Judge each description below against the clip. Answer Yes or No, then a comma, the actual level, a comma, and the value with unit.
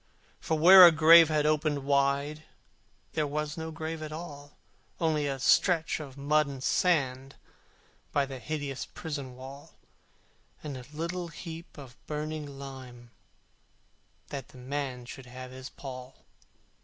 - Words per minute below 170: Yes, average, 140 wpm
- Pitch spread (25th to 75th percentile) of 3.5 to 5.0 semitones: No, average, 2.7 semitones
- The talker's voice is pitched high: No, medium, 145 Hz